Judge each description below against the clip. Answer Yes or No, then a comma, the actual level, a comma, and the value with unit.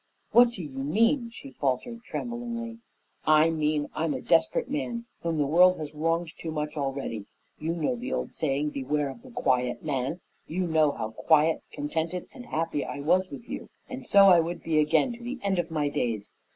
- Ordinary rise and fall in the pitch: No, wide, 7.6 semitones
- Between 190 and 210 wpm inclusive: Yes, average, 195 wpm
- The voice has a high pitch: No, medium, 160 Hz